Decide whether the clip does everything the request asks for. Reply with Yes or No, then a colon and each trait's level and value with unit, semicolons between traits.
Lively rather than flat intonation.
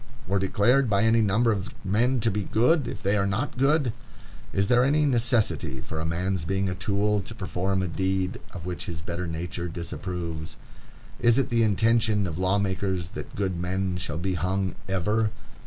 No: average, 3.7 semitones